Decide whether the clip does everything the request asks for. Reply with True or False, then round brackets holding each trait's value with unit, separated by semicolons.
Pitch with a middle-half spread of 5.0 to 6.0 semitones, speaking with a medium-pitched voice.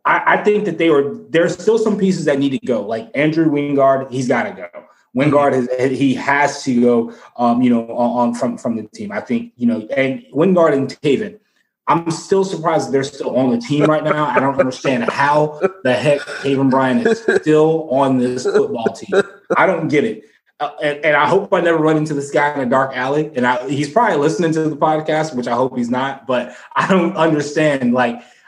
False (3.8 semitones; 145 Hz)